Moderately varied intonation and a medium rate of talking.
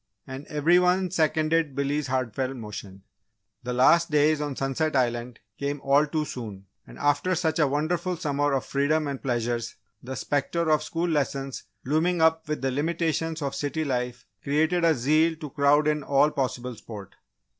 Yes: average, 3.2 semitones; average, 165 wpm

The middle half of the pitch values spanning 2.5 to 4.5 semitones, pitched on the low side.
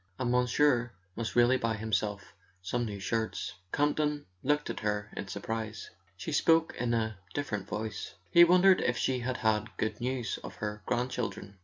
Yes: average, 3.4 semitones; low, 120 Hz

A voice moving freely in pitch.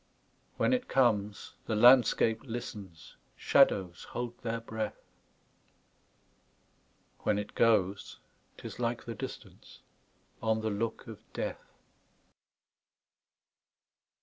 No: narrow, 2.4 semitones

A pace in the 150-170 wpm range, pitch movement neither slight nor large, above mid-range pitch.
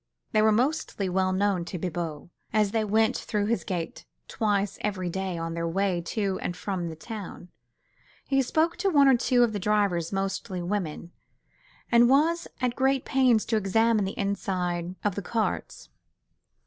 Yes: average, 160 wpm; average, 4.2 semitones; high, 200 Hz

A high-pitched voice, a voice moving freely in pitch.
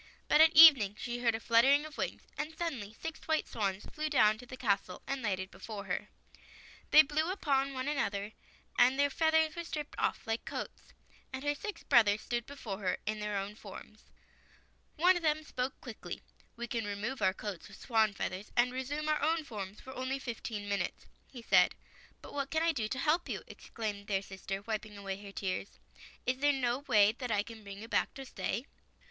Yes: high, 240 Hz; wide, 5.8 semitones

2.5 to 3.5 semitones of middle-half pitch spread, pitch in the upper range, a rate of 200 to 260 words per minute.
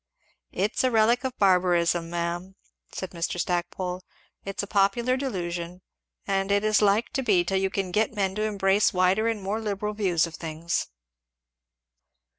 No: average, 3.1 semitones; high, 195 Hz; average, 160 wpm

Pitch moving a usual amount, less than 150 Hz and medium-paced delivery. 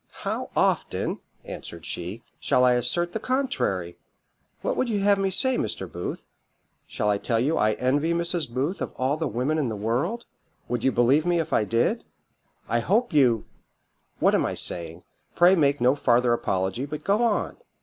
No: wide, 7.1 semitones; low, 135 Hz; average, 180 wpm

